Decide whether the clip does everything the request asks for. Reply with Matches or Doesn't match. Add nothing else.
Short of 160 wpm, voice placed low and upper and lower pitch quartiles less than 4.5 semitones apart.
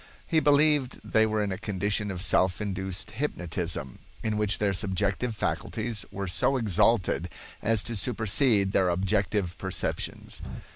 Matches